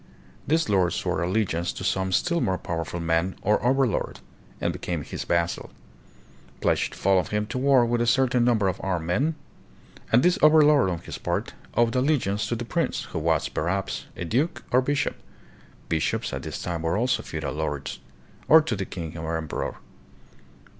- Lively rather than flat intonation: Yes, wide, 6.7 semitones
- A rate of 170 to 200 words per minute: Yes, average, 180 wpm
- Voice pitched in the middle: No, low, 105 Hz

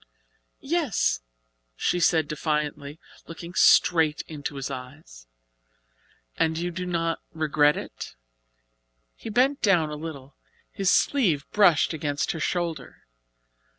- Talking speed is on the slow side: Yes, slow, 115 wpm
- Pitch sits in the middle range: Yes, medium, 160 Hz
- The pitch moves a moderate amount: Yes, average, 3.2 semitones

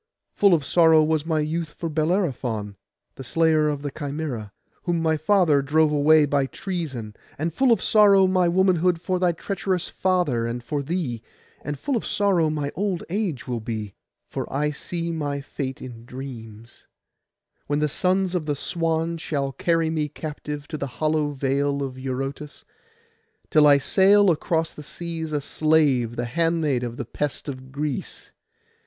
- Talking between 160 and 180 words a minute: Yes, average, 165 wpm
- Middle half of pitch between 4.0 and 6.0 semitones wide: No, average, 3.5 semitones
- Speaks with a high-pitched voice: No, medium, 155 Hz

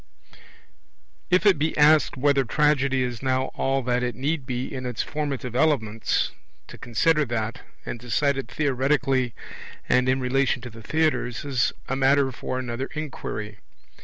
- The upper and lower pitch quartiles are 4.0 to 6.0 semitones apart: No, average, 2.8 semitones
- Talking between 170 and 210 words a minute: No, average, 155 wpm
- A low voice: Yes, low, 130 Hz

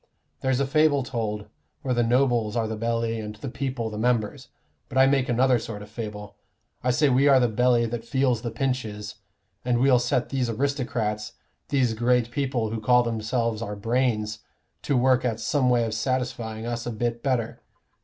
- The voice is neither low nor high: No, low, 120 Hz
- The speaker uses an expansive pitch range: No, narrow, 2.5 semitones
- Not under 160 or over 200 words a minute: Yes, average, 185 wpm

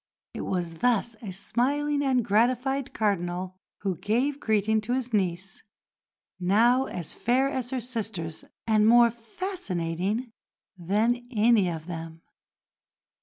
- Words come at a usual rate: No, slow, 125 wpm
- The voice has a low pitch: No, high, 220 Hz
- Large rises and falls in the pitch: No, average, 5.0 semitones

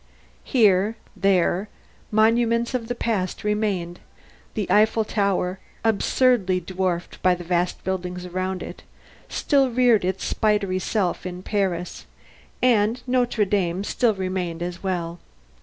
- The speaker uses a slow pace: Yes, slow, 125 wpm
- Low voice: No, high, 195 Hz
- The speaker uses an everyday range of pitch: Yes, average, 3.5 semitones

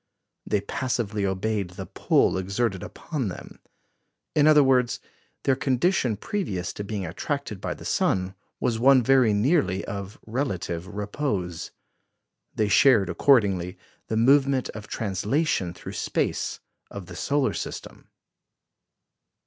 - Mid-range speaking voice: No, low, 110 Hz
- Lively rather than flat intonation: Yes, wide, 5.7 semitones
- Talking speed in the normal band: No, slow, 125 wpm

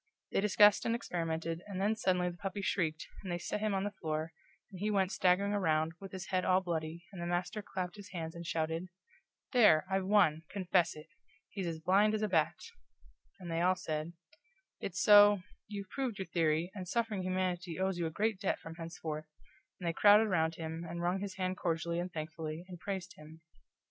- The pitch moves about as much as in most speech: Yes, average, 3.1 semitones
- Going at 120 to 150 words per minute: No, fast, 205 wpm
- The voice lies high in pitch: No, medium, 180 Hz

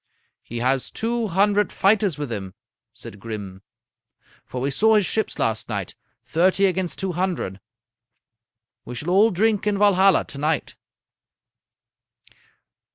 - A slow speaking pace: Yes, slow, 130 wpm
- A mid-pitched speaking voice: Yes, medium, 180 Hz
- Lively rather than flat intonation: Yes, wide, 8.6 semitones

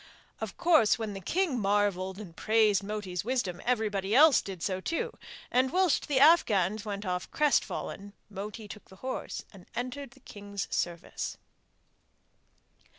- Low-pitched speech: No, high, 210 Hz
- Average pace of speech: Yes, average, 145 wpm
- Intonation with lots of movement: No, average, 4.7 semitones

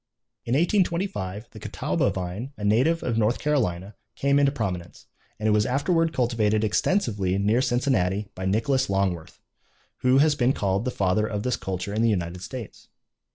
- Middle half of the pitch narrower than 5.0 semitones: No, wide, 5.4 semitones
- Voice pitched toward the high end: No, low, 110 Hz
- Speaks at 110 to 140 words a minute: No, average, 165 wpm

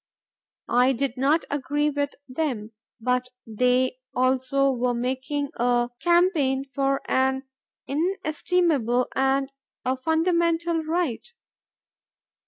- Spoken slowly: Yes, slow, 95 wpm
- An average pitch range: Yes, average, 3.7 semitones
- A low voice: No, very high, 270 Hz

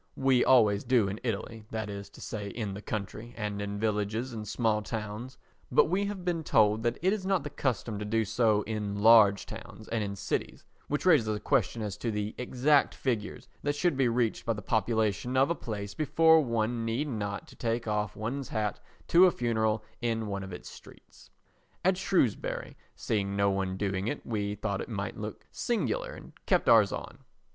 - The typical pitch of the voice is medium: No, low, 110 Hz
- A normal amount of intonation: Yes, average, 3.3 semitones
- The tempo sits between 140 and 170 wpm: No, average, 195 wpm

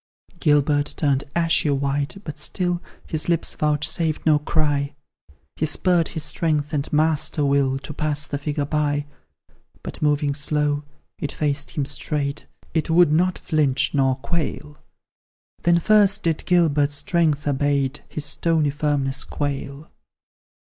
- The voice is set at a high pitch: No, medium, 150 Hz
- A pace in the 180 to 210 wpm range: No, slow, 135 wpm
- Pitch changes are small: Yes, narrow, 1.9 semitones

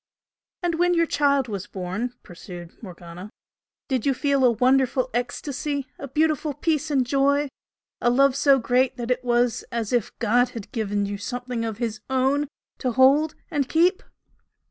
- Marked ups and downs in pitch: No, average, 3.5 semitones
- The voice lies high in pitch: Yes, very high, 255 Hz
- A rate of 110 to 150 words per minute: No, average, 165 wpm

